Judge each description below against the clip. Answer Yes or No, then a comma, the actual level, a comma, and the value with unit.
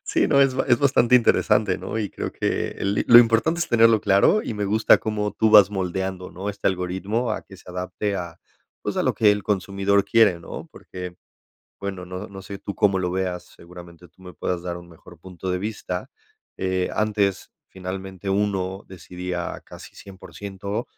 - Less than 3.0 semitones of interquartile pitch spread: Yes, narrow, 2.4 semitones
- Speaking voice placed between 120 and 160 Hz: No, very low, 95 Hz